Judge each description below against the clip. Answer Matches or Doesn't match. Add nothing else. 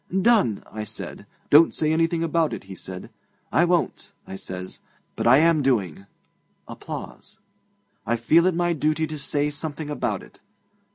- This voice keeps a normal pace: Matches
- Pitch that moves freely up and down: Matches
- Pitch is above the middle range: Doesn't match